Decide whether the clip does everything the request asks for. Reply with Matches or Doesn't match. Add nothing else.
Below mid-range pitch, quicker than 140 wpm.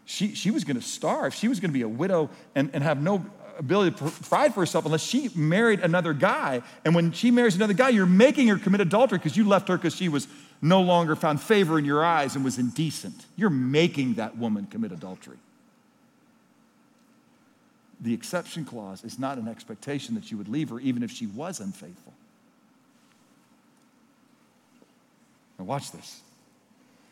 Doesn't match